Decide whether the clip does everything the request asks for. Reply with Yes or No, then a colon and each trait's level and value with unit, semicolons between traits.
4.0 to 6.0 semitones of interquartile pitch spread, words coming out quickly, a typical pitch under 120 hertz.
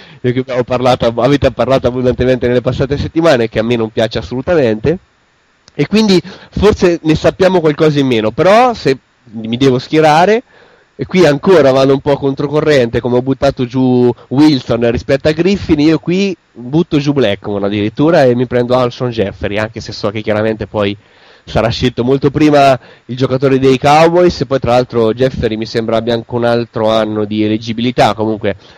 No: average, 4.3 semitones; fast, 175 wpm; low, 125 Hz